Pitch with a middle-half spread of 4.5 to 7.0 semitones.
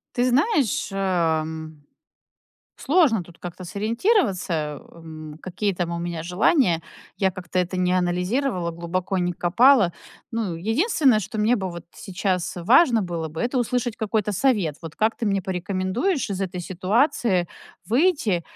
Yes: average, 5.0 semitones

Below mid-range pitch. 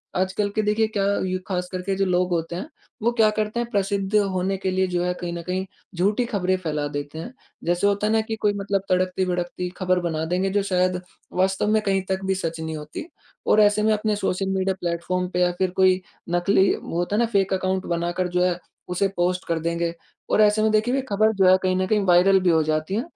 No: medium, 185 Hz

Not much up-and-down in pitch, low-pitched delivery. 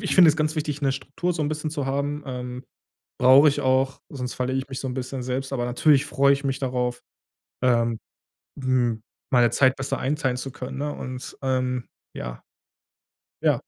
Yes: narrow, 2.1 semitones; low, 130 Hz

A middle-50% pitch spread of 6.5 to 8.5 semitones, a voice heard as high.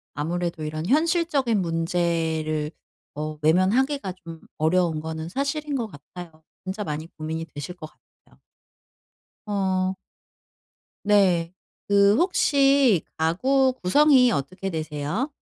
No: wide, 7.3 semitones; medium, 180 Hz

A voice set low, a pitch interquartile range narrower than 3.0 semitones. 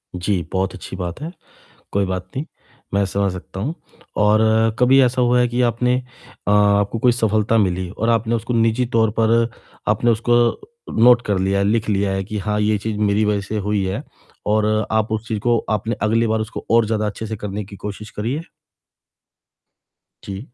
Yes: low, 105 Hz; narrow, 2.4 semitones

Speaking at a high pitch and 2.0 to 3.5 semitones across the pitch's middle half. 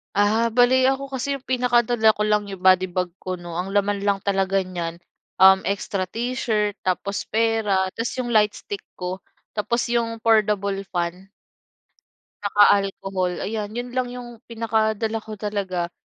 Yes: high, 205 Hz; average, 3.1 semitones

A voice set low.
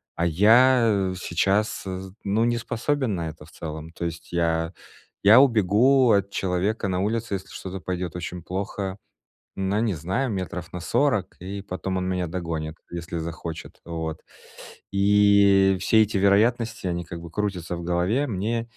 Yes: very low, 95 Hz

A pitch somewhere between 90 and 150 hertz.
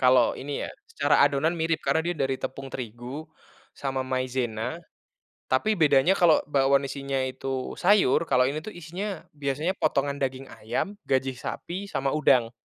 Yes: medium, 140 Hz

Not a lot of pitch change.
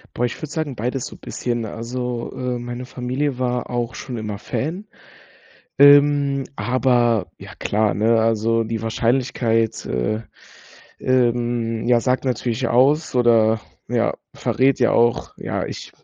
Yes: narrow, 2.2 semitones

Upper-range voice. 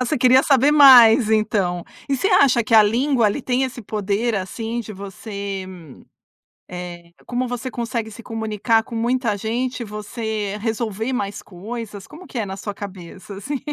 Yes: high, 225 Hz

